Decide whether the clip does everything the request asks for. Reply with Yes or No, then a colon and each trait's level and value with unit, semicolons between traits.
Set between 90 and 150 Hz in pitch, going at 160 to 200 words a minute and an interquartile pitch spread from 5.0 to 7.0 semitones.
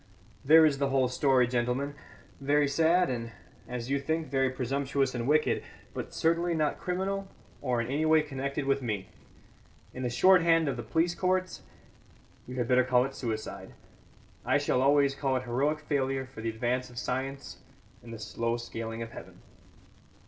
No: low, 135 Hz; average, 175 wpm; average, 3.5 semitones